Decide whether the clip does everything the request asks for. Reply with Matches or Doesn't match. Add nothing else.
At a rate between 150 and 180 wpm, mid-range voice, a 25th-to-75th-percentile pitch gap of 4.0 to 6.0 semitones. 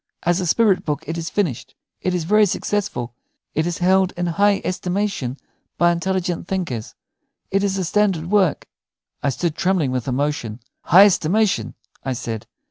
Matches